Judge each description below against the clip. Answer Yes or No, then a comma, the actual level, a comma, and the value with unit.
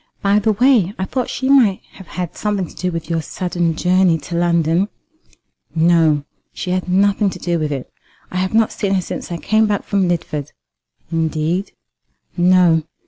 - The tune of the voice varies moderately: Yes, average, 3.1 semitones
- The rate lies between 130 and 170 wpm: No, average, 185 wpm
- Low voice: No, medium, 180 Hz